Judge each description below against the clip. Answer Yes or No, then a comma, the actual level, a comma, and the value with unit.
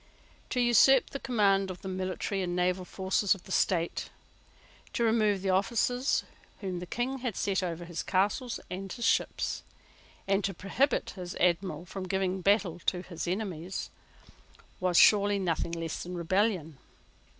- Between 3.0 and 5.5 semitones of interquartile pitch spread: No, narrow, 2.5 semitones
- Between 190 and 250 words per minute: No, average, 155 wpm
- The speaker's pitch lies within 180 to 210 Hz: Yes, high, 190 Hz